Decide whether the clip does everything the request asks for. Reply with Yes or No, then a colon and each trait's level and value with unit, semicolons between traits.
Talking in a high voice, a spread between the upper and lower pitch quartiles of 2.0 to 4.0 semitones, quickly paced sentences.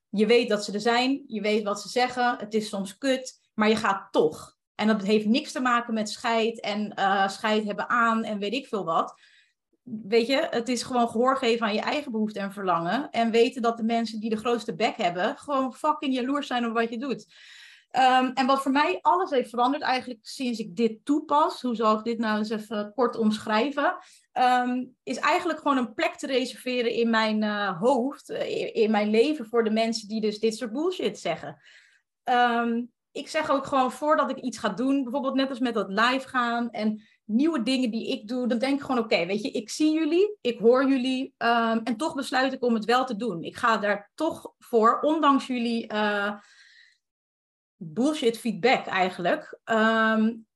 Yes: high, 235 Hz; average, 3.2 semitones; fast, 205 wpm